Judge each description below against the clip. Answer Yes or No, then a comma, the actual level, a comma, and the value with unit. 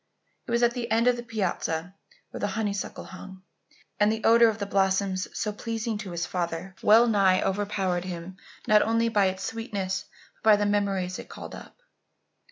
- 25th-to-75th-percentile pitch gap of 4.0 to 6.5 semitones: No, average, 3.0 semitones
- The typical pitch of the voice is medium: No, high, 205 Hz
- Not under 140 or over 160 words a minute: No, average, 190 wpm